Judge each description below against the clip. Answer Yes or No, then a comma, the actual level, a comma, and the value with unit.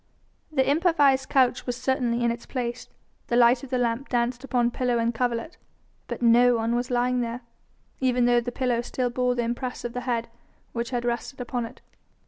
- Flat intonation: Yes, narrow, 1.1 semitones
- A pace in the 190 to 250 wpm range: Yes, average, 195 wpm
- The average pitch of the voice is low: No, high, 245 Hz